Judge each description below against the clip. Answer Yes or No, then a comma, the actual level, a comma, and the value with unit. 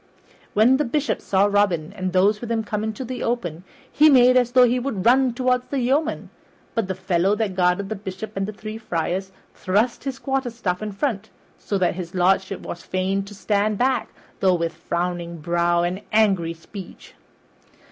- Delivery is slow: No, average, 190 wpm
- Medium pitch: No, high, 205 Hz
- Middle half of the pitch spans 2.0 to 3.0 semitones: No, average, 4.6 semitones